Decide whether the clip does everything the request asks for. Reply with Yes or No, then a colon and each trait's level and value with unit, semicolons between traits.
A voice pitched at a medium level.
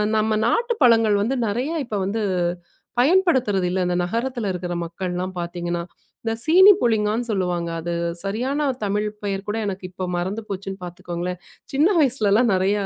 No: high, 205 Hz